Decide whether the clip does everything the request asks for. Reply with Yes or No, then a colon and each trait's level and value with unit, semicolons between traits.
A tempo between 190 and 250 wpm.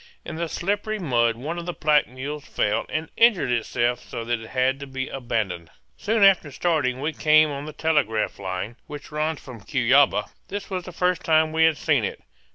Yes: average, 200 wpm